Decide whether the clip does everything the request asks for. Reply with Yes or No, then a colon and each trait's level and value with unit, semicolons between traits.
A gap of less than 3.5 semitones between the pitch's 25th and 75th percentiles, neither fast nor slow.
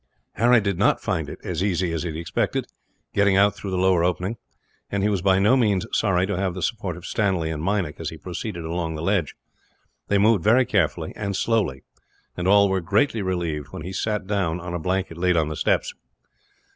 No: average, 3.0 semitones; fast, 215 wpm